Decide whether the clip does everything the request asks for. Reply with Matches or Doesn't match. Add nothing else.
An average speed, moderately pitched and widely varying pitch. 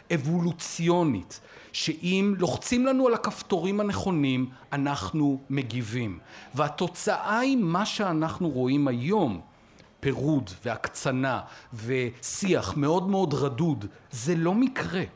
Doesn't match